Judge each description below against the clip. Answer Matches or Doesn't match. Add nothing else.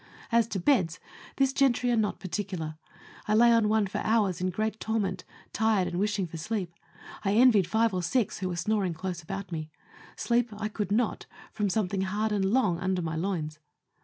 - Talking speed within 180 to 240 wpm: Matches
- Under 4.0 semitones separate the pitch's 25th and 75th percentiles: Matches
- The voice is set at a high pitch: Matches